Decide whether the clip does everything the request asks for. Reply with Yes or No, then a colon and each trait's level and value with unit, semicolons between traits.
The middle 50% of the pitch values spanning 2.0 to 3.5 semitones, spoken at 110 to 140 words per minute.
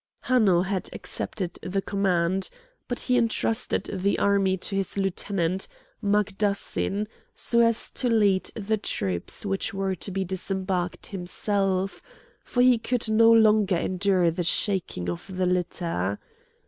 Yes: narrow, 2.6 semitones; slow, 135 wpm